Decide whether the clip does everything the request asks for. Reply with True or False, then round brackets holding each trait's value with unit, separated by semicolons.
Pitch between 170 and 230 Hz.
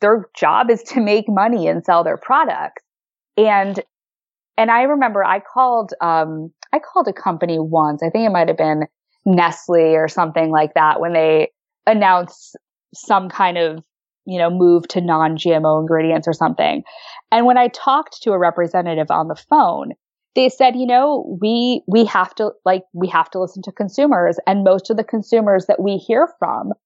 True (190 Hz)